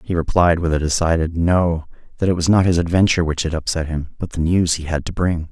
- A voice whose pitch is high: No, very low, 85 Hz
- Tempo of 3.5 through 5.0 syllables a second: No, 5.9 syllables/s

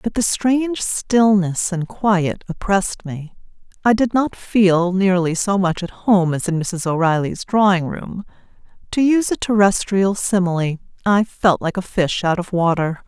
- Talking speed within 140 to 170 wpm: Yes, average, 160 wpm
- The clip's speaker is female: Yes, female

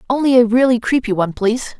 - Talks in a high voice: Yes, high, 235 Hz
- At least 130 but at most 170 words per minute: No, average, 200 wpm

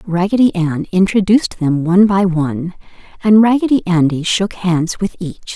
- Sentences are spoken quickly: No, average, 150 wpm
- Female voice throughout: Yes, female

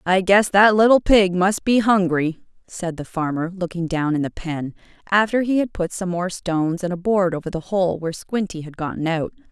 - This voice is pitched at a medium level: Yes, medium, 180 Hz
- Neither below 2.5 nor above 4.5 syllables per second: No, 5.1 syllables/s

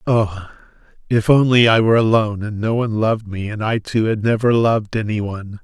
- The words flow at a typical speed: Yes, average, 190 wpm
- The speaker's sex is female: No, male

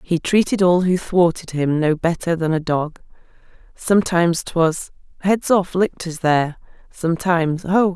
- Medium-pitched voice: Yes, medium, 170 Hz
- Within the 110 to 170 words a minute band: Yes, average, 145 wpm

